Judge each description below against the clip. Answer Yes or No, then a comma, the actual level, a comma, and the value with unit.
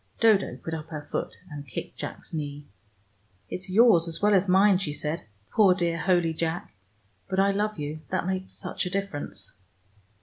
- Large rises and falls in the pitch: No, average, 4.0 semitones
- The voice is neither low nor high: Yes, medium, 175 Hz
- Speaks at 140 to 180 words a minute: Yes, average, 175 wpm